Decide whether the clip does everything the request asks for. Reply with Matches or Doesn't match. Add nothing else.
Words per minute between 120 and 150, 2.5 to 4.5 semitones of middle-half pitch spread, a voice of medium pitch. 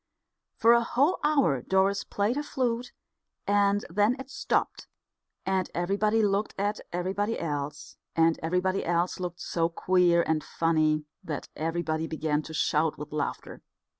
Matches